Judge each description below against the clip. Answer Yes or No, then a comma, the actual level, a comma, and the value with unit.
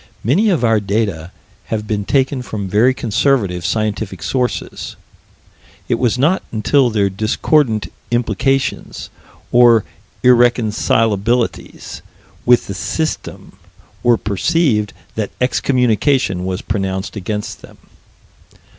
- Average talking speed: No, slow, 100 wpm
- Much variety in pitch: No, average, 3.7 semitones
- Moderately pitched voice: No, low, 115 Hz